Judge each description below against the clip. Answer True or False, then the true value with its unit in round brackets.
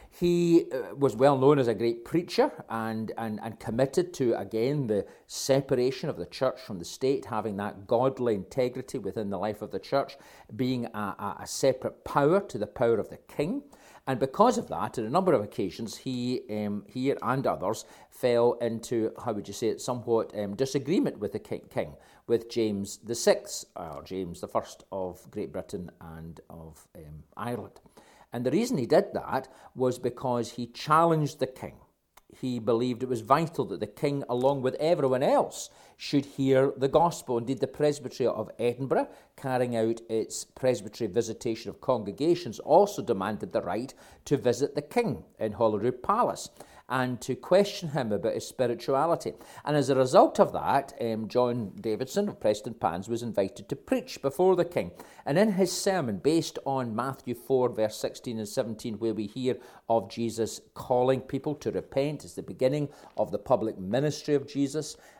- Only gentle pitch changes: False (3.8 semitones)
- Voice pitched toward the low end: True (125 Hz)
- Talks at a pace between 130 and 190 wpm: True (180 wpm)